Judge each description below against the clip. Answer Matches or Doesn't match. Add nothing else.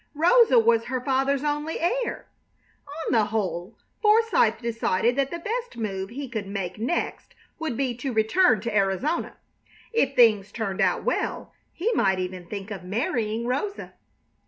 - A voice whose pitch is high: Matches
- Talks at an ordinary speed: Matches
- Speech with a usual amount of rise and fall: Doesn't match